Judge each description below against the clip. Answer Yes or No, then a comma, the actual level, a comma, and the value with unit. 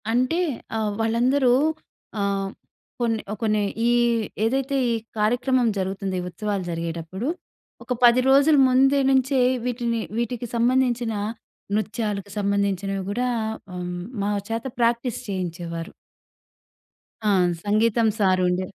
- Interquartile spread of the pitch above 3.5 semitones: Yes, average, 4.0 semitones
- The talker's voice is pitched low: No, high, 225 Hz